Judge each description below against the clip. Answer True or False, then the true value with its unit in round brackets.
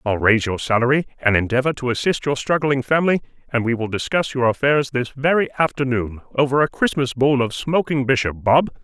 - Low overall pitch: True (130 Hz)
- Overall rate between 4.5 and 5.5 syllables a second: False (5.7 syllables/s)